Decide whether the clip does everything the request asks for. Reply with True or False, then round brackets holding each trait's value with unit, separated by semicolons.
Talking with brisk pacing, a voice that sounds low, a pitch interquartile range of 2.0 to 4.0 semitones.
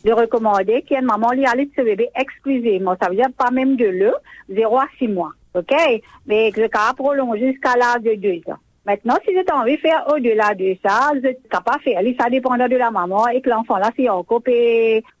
False (240 wpm; 245 Hz; 3.2 semitones)